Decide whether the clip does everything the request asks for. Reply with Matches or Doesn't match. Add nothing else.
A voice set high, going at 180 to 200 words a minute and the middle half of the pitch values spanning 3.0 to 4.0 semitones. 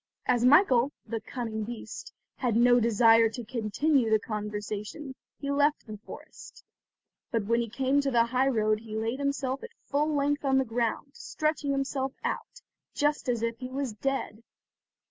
Doesn't match